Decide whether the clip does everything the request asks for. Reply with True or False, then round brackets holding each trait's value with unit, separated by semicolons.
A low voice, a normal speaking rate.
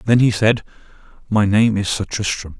True (105 Hz; 185 wpm)